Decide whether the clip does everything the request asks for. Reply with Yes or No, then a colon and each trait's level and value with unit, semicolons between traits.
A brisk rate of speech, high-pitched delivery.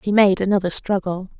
No: average, 170 wpm; high, 195 Hz